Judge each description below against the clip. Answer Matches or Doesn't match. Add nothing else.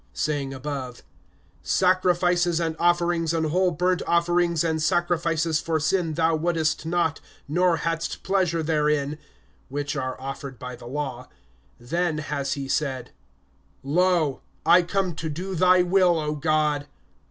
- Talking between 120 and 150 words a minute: Matches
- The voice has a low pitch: Doesn't match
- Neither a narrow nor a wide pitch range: Matches